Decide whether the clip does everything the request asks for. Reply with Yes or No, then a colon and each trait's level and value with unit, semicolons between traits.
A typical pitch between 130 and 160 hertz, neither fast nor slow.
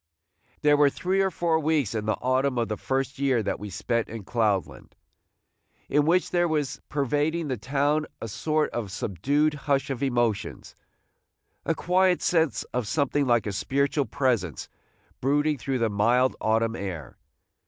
Yes: low, 135 Hz; average, 165 wpm